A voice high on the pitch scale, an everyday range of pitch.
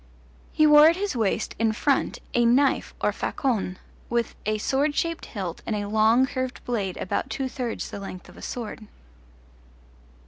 Yes: high, 235 Hz; average, 4.3 semitones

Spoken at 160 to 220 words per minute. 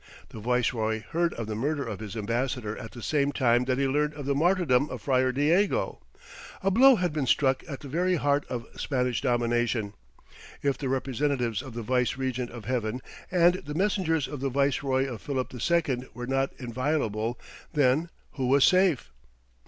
Yes: average, 180 wpm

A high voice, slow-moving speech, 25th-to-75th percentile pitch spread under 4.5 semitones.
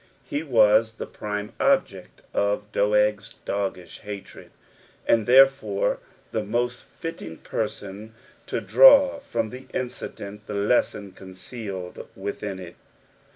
No: low, 105 Hz; slow, 105 wpm; average, 3.4 semitones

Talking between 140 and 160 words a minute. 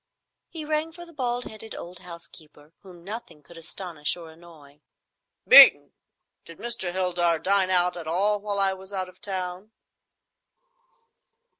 Yes: average, 145 wpm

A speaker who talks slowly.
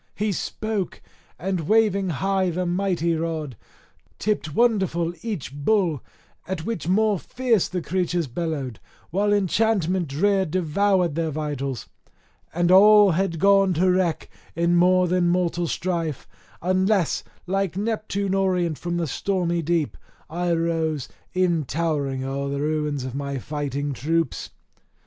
Yes: slow, 130 wpm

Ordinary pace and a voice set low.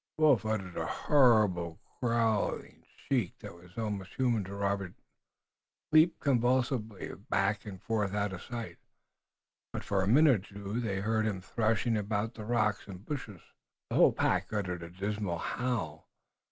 Yes: average, 155 wpm; low, 105 Hz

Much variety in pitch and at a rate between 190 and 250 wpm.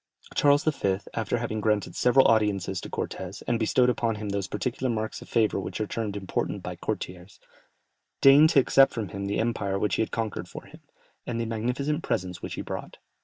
No: average, 3.6 semitones; average, 200 wpm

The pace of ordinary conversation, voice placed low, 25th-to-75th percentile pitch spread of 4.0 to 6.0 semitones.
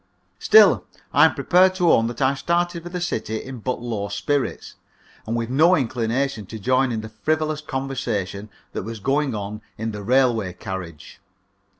Yes: average, 175 wpm; low, 125 Hz; average, 5.1 semitones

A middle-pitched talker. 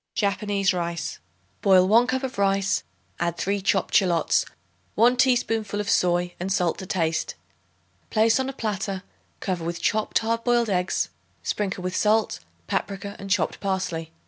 No: high, 195 Hz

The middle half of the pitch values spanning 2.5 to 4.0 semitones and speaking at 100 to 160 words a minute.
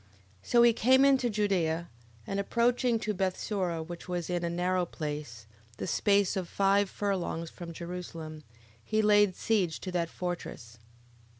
Yes: average, 3.5 semitones; average, 155 wpm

